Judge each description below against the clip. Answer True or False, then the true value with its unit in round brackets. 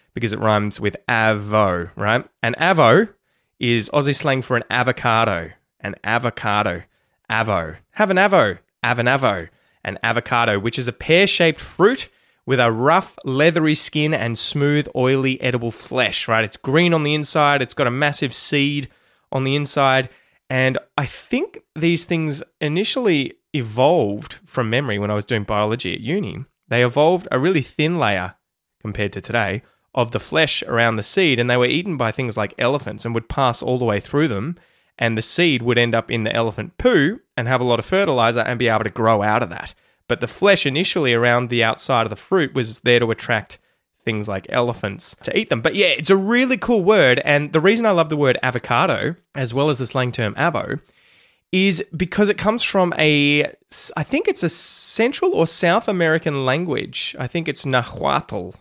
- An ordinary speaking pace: True (190 wpm)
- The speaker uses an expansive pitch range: True (5.7 semitones)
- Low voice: True (130 Hz)